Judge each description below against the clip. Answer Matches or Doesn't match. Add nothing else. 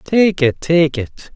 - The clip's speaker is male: Matches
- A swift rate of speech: Doesn't match